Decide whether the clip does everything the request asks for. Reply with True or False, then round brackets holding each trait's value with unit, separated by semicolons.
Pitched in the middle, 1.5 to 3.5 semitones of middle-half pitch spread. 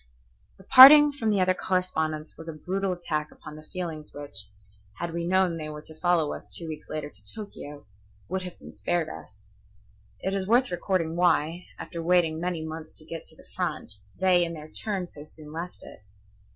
True (170 Hz; 3.0 semitones)